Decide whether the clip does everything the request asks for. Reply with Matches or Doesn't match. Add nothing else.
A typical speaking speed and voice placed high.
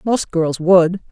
Doesn't match